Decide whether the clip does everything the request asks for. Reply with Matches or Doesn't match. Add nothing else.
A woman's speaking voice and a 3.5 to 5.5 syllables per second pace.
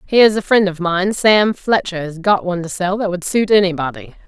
Doesn't match